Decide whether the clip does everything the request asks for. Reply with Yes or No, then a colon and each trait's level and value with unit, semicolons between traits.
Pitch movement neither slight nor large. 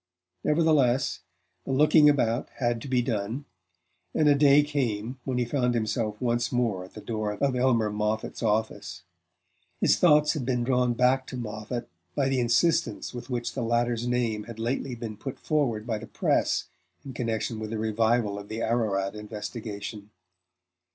Yes: average, 3.1 semitones